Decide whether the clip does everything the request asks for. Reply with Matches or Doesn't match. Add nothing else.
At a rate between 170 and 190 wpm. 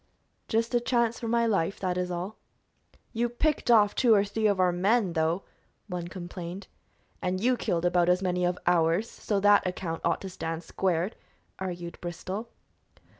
Matches